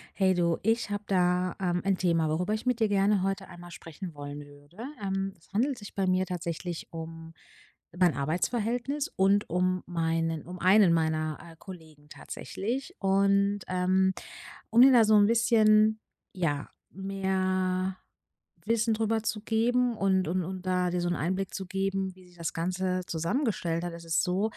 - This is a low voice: No, medium, 185 Hz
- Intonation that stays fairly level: No, average, 3.1 semitones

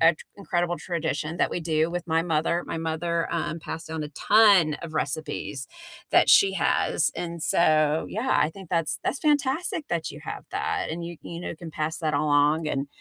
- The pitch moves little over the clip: Yes, narrow, 2.0 semitones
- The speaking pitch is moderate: Yes, medium, 165 Hz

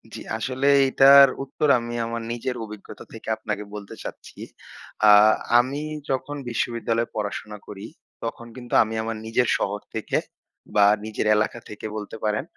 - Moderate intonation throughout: Yes, average, 3.1 semitones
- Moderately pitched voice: No, low, 115 Hz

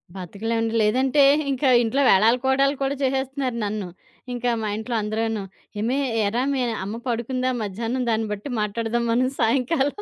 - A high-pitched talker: Yes, high, 235 Hz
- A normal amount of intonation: Yes, average, 3.2 semitones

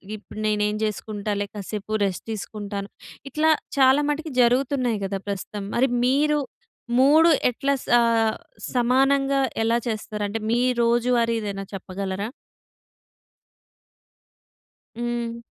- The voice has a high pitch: Yes, high, 230 Hz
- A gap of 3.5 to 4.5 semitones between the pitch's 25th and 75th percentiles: Yes, average, 4.1 semitones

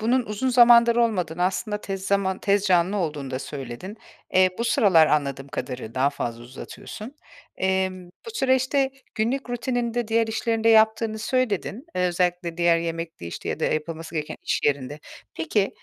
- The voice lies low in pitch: No, high, 190 Hz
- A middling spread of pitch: No, wide, 6.0 semitones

